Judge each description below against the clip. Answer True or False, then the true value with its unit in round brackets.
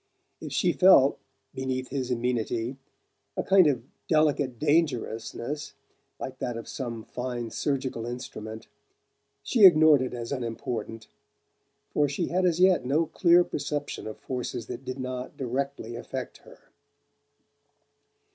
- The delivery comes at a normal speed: False (130 wpm)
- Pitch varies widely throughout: False (3.8 semitones)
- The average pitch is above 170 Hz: False (130 Hz)